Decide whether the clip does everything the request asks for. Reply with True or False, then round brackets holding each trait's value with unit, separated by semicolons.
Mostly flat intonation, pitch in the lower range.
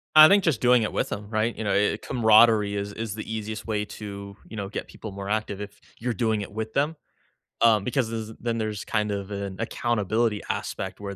True (2.0 semitones; 110 Hz)